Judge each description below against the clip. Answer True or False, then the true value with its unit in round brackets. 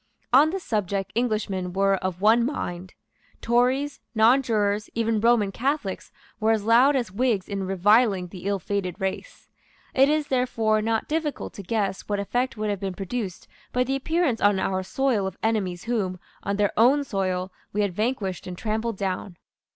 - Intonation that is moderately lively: True (4.1 semitones)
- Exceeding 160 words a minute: True (170 wpm)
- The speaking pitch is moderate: False (215 Hz)